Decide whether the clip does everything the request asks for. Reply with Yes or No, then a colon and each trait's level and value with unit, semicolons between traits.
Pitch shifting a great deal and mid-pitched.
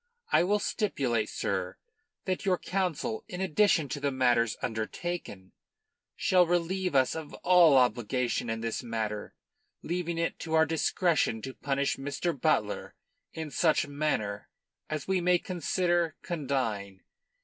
Yes: wide, 6.2 semitones; medium, 155 Hz